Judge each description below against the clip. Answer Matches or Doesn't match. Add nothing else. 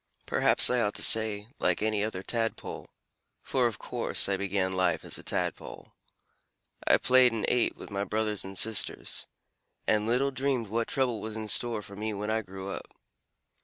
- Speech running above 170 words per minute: Matches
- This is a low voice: Matches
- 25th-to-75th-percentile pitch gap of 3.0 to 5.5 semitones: Doesn't match